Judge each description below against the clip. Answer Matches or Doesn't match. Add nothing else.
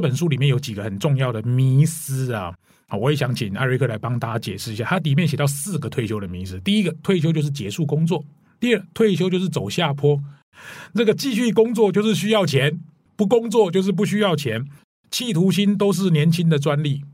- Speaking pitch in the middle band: Matches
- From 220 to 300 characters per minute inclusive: Doesn't match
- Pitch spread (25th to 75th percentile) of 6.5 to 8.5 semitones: Matches